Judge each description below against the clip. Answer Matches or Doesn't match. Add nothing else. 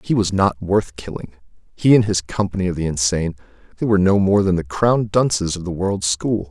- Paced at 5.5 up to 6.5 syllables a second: Matches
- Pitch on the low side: Matches